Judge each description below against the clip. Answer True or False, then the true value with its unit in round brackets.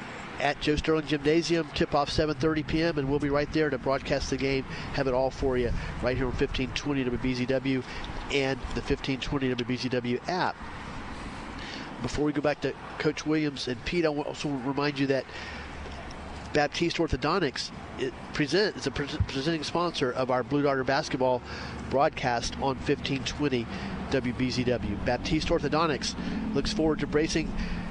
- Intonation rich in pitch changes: False (3.1 semitones)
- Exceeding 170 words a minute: False (150 wpm)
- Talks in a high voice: False (135 Hz)